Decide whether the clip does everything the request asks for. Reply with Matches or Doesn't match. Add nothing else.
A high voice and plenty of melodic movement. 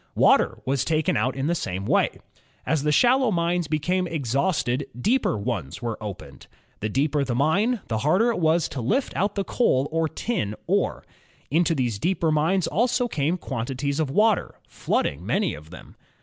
Doesn't match